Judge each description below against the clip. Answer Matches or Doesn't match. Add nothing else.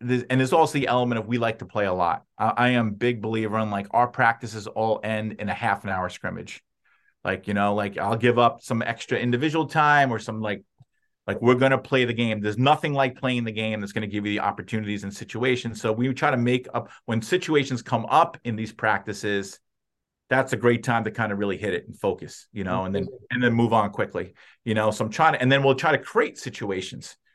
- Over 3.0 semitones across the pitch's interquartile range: Doesn't match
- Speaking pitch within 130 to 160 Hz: Doesn't match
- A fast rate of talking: Matches